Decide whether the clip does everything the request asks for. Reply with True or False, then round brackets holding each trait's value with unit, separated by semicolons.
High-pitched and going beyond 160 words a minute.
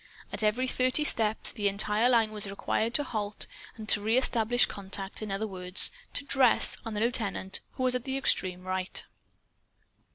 True (215 Hz; 170 wpm)